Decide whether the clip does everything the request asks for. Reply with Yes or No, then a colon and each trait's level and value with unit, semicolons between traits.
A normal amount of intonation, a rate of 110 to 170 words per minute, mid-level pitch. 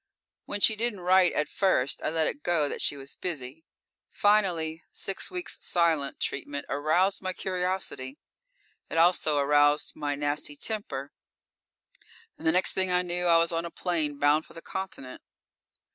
Yes: average, 4.2 semitones; average, 160 wpm; medium, 165 Hz